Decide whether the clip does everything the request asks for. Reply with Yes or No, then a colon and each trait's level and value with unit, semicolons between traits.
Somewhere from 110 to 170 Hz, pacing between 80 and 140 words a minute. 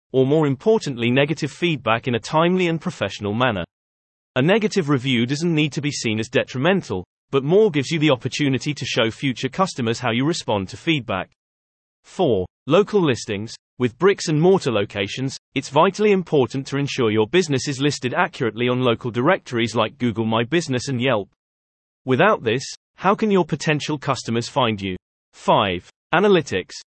No: low, 135 Hz; average, 165 wpm